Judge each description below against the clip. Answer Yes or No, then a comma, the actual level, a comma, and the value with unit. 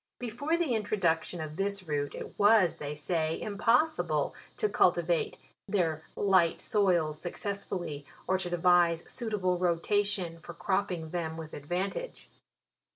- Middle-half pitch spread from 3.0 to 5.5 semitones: Yes, average, 4.0 semitones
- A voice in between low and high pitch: Yes, medium, 180 Hz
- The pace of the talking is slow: Yes, slow, 130 wpm